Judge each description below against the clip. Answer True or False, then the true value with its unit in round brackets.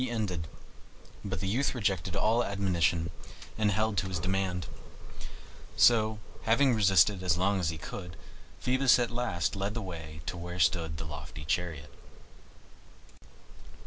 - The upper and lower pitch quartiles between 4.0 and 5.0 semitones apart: True (4.4 semitones)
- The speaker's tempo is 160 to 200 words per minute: False (145 wpm)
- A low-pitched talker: True (95 Hz)